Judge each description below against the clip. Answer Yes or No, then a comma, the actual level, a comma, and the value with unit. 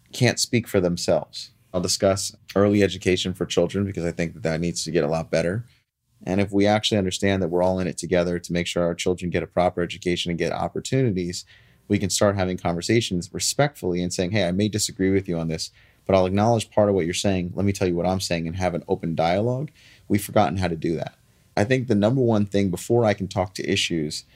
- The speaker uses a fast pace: Yes, fast, 240 wpm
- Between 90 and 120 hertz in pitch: Yes, very low, 95 Hz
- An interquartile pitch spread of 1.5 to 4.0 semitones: Yes, average, 2.9 semitones